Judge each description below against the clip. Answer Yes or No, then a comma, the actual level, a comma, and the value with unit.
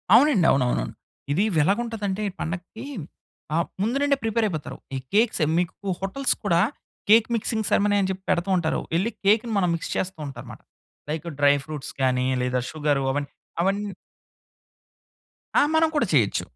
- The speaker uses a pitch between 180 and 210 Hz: Yes, high, 190 Hz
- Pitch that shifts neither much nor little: No, wide, 6.3 semitones